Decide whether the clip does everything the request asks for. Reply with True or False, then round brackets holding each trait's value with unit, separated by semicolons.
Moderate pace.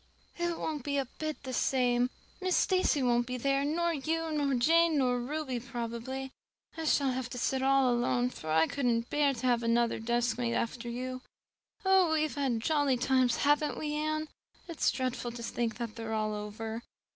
True (180 wpm)